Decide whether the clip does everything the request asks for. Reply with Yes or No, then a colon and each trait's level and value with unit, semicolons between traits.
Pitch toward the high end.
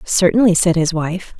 No: medium, 180 Hz